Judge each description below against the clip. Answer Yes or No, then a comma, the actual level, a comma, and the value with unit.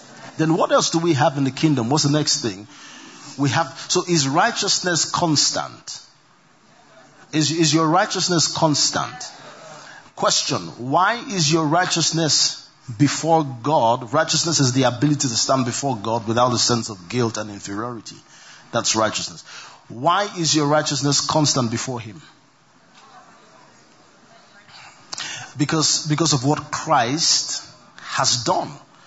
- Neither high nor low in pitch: Yes, medium, 150 Hz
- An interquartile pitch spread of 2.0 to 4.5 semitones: Yes, average, 4.1 semitones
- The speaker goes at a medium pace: No, slow, 130 wpm